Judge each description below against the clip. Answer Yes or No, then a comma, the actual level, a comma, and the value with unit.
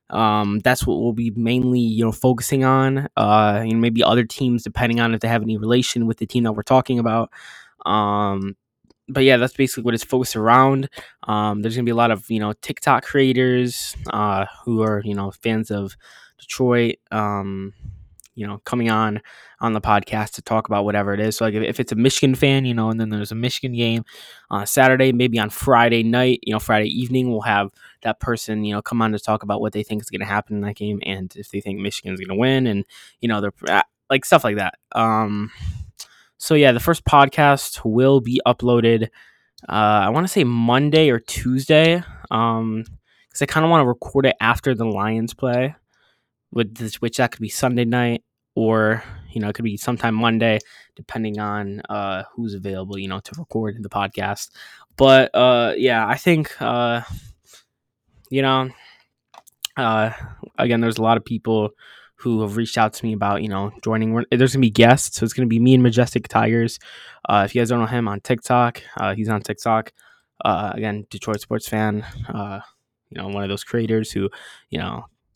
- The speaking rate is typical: No, fast, 210 wpm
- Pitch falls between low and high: No, low, 115 Hz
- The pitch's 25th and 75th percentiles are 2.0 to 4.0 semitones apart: Yes, average, 2.8 semitones